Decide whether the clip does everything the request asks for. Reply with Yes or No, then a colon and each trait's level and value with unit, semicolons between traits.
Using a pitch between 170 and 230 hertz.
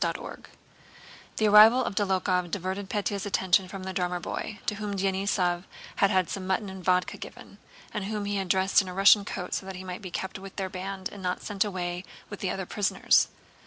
Yes: high, 190 Hz